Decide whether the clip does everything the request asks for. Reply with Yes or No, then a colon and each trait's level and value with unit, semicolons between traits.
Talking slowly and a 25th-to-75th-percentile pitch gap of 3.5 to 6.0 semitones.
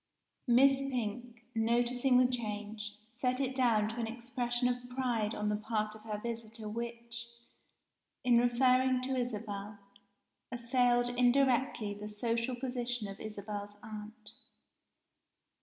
No: slow, 125 wpm; narrow, 2.6 semitones